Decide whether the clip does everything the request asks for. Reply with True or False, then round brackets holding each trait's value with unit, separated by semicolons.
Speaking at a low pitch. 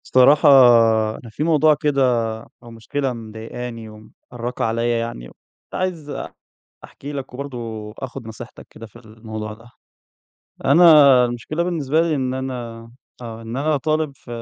True (125 Hz)